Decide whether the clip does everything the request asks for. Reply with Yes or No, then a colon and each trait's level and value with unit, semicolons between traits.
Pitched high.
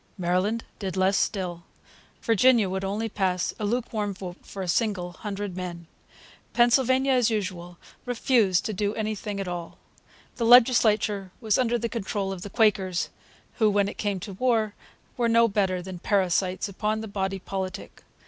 Yes: high, 205 Hz